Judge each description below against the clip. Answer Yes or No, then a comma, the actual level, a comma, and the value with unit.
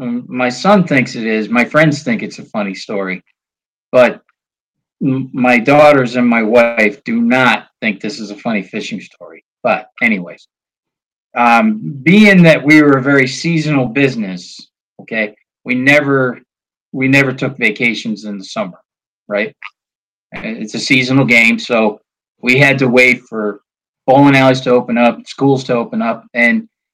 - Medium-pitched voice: No, low, 125 Hz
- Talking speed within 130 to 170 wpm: Yes, average, 155 wpm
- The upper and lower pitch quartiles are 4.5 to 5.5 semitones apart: No, average, 3.3 semitones